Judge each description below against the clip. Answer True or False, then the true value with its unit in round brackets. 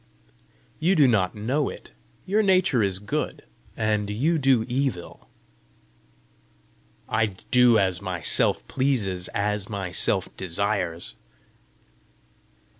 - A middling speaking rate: False (115 wpm)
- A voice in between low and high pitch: False (105 Hz)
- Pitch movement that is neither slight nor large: False (5.7 semitones)